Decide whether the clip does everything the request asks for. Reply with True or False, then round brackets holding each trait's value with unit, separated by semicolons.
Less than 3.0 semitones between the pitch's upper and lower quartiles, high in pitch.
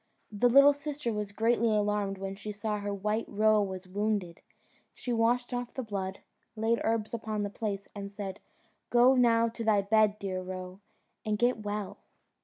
True (2.4 semitones; 210 Hz)